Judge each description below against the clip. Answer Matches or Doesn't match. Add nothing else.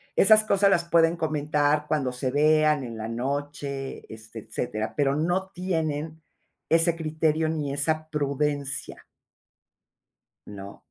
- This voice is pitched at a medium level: Matches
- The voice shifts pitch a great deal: Doesn't match